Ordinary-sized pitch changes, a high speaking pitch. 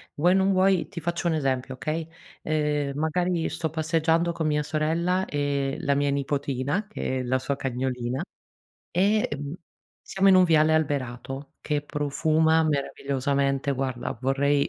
No: average, 3.0 semitones; medium, 150 Hz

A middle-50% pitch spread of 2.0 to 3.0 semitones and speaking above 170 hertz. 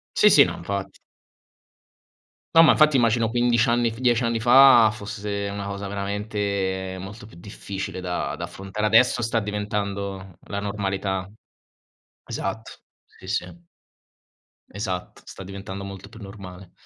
No: narrow, 2.6 semitones; low, 100 Hz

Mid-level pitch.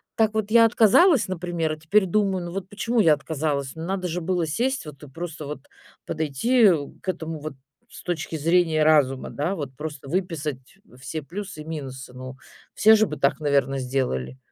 Yes: medium, 160 Hz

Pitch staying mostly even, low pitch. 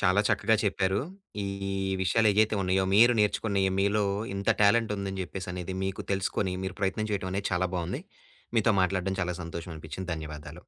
Yes: narrow, 1.9 semitones; very low, 95 Hz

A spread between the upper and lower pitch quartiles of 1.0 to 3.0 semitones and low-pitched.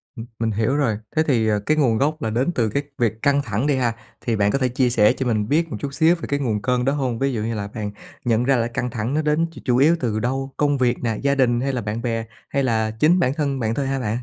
No: average, 3.8 semitones; low, 125 Hz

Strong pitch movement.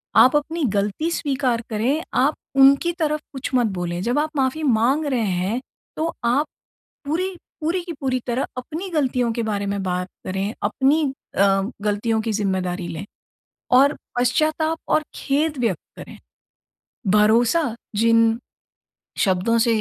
Yes: wide, 6.1 semitones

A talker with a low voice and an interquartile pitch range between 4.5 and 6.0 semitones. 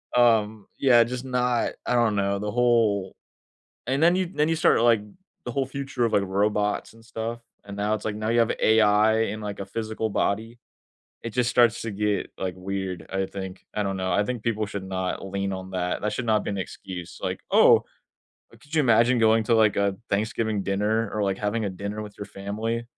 No: low, 110 Hz; average, 2.8 semitones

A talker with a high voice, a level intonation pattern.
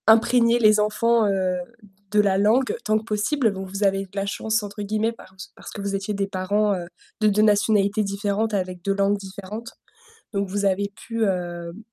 Yes: high, 205 Hz; narrow, 1.7 semitones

